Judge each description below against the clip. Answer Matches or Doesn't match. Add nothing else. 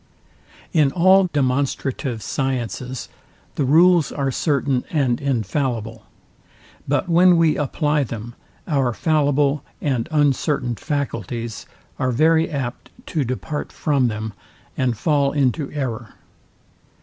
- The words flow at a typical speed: Doesn't match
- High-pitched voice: Doesn't match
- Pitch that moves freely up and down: Doesn't match